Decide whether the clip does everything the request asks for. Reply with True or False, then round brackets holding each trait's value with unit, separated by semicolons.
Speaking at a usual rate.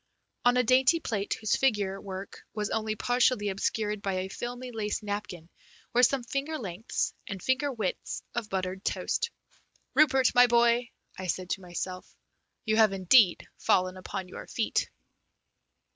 True (150 wpm)